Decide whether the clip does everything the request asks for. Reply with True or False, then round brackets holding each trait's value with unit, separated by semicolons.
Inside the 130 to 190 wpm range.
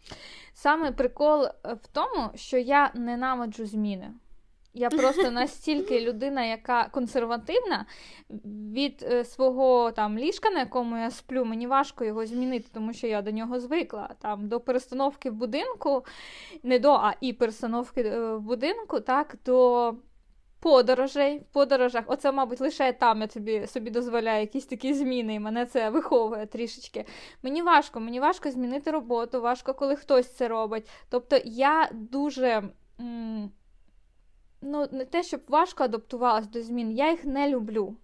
True (145 wpm)